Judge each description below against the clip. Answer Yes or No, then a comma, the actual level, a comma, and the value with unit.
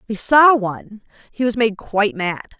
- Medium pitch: No, high, 220 Hz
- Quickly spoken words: Yes, fast, 210 wpm